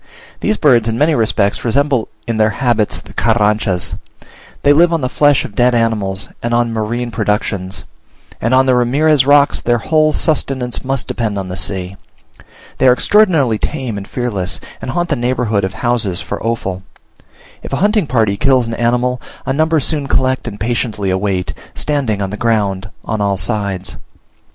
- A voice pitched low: Yes, low, 120 Hz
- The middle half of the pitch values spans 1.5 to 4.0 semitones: No, average, 4.4 semitones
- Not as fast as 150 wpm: No, average, 175 wpm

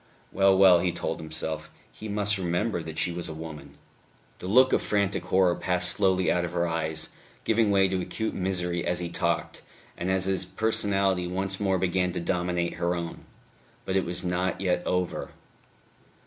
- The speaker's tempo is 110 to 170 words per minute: No, average, 180 wpm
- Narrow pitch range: Yes, narrow, 1.8 semitones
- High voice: No, very low, 90 Hz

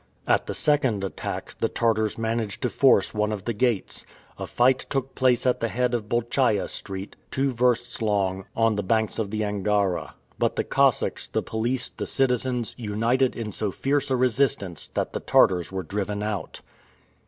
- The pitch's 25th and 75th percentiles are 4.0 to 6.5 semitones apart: No, average, 3.4 semitones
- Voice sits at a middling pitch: No, low, 115 Hz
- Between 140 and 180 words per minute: Yes, average, 175 wpm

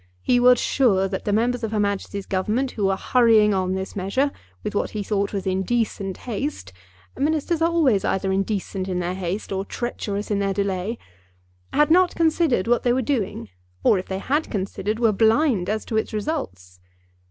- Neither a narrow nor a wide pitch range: Yes, average, 4.4 semitones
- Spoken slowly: No, average, 185 wpm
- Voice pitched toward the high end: Yes, high, 210 Hz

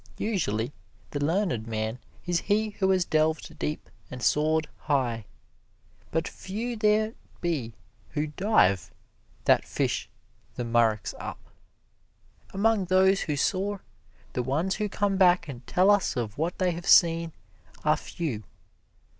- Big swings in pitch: Yes, wide, 7.1 semitones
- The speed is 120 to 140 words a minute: Yes, slow, 135 wpm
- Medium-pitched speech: Yes, medium, 165 Hz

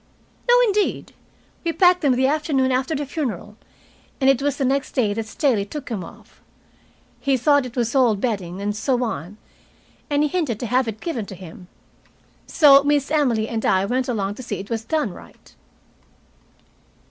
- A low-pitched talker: No, very high, 255 Hz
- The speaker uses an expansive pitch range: No, average, 4.9 semitones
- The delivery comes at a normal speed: Yes, average, 180 wpm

